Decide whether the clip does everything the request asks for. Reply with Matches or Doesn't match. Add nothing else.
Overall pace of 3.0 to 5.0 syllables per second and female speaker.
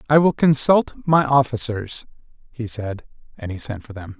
Doesn't match